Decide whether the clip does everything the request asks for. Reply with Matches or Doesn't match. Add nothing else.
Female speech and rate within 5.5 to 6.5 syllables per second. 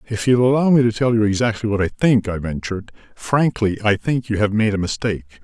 Doesn't match